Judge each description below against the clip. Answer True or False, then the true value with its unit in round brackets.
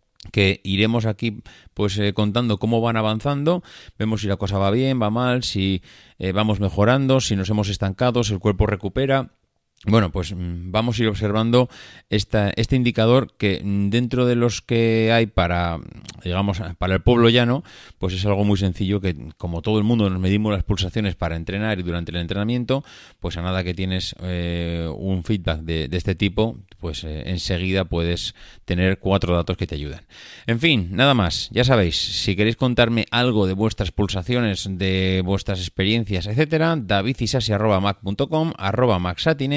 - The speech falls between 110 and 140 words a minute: False (165 wpm)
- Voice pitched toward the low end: True (105 Hz)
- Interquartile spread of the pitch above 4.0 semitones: False (3.7 semitones)